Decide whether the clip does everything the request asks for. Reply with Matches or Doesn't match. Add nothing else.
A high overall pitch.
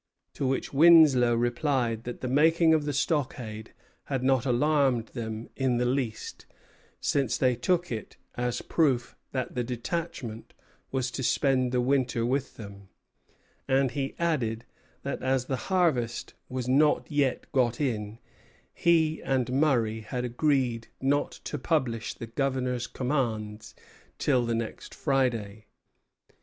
Doesn't match